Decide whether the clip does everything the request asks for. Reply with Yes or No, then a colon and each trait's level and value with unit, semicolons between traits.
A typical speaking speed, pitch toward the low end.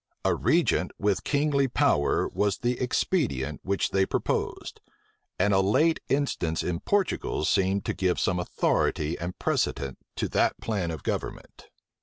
Yes: average, 145 wpm; very low, 95 Hz